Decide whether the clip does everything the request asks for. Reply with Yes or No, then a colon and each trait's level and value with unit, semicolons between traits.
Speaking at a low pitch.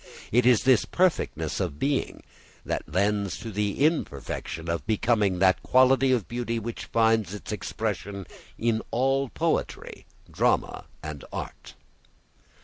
Yes: low, 110 Hz